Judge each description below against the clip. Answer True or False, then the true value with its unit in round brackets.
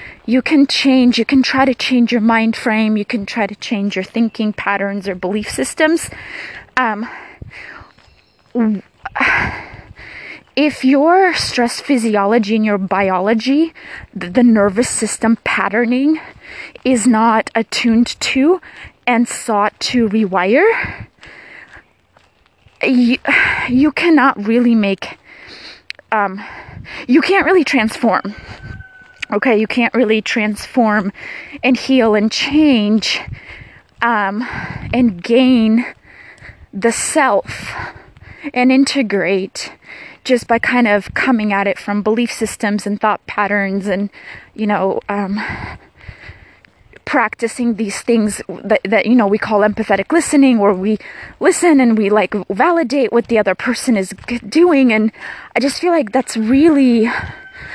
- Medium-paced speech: False (120 wpm)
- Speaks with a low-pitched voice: False (230 Hz)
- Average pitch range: True (4.1 semitones)